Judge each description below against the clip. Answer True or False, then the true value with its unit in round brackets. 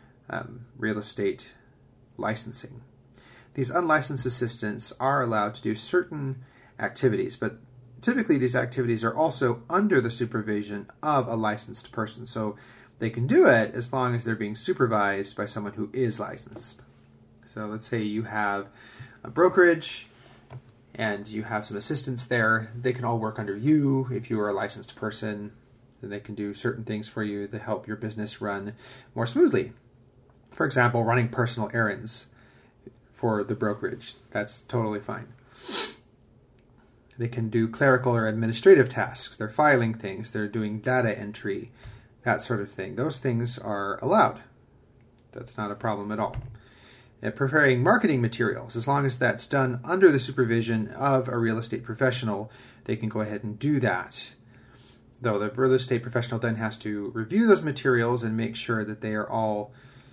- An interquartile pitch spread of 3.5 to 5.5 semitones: False (2.8 semitones)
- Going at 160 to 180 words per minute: True (165 wpm)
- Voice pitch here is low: True (120 Hz)